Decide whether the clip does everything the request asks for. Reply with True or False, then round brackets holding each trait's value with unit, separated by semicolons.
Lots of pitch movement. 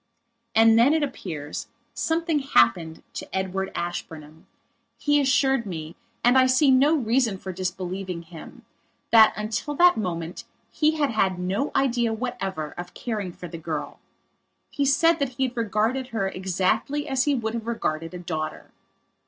True (7.0 semitones)